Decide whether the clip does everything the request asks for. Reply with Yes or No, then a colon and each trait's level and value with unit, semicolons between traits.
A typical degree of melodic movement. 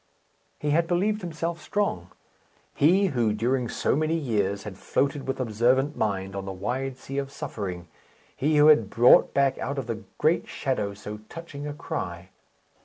No: wide, 6.4 semitones